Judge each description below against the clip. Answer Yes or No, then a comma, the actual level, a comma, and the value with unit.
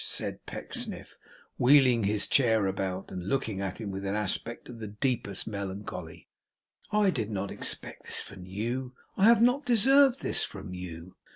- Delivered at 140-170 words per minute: Yes, average, 165 wpm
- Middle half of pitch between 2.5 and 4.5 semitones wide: No, wide, 5.6 semitones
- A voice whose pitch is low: Yes, low, 105 Hz